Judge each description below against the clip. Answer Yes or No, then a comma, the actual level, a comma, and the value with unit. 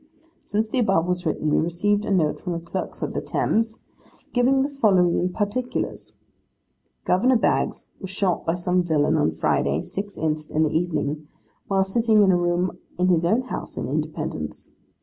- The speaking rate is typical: Yes, average, 175 wpm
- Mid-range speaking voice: Yes, medium, 180 Hz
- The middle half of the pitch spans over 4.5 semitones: No, average, 3.9 semitones